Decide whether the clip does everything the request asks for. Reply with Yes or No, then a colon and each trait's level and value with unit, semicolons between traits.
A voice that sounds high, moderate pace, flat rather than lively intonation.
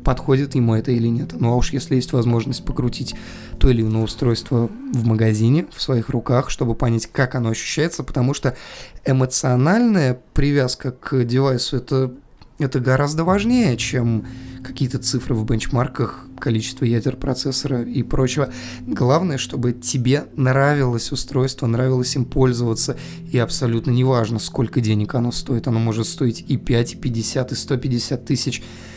No: low, 130 Hz; average, 145 wpm; narrow, 2.2 semitones